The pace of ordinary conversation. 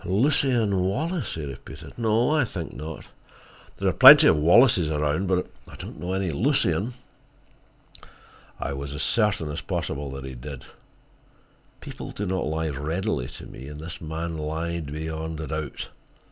Yes: average, 160 wpm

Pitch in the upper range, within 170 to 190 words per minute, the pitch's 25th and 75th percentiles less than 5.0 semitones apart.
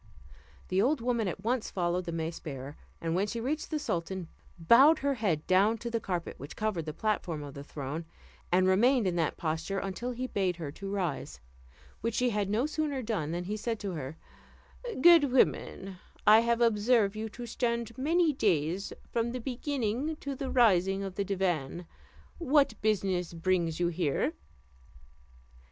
No: high, 200 Hz; average, 175 wpm; wide, 5.5 semitones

